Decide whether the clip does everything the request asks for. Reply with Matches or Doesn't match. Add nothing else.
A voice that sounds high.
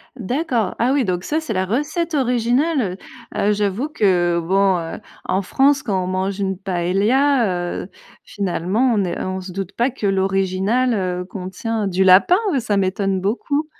Matches